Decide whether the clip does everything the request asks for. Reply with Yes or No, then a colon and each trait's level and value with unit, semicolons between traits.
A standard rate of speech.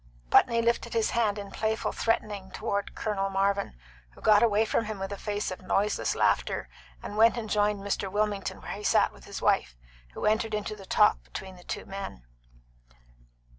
Yes: average, 180 wpm